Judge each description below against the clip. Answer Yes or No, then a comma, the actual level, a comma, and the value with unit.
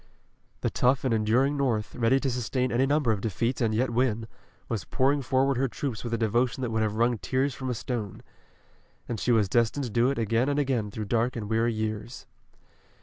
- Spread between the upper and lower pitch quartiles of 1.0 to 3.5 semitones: Yes, average, 2.8 semitones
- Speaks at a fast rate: Yes, fast, 210 wpm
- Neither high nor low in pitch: No, low, 120 Hz